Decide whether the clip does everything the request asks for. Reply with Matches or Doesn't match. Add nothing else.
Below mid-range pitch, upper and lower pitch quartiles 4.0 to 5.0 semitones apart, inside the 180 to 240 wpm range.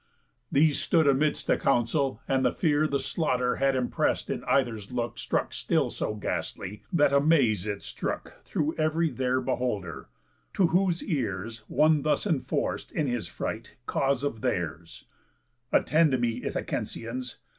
Doesn't match